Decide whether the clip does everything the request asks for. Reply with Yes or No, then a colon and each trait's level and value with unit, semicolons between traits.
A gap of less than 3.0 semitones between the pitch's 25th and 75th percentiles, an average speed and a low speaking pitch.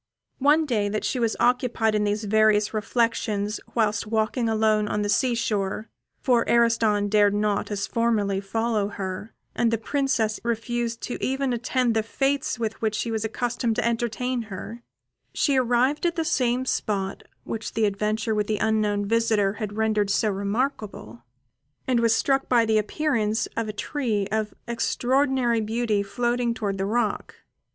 No: narrow, 2.4 semitones; average, 160 wpm; high, 225 Hz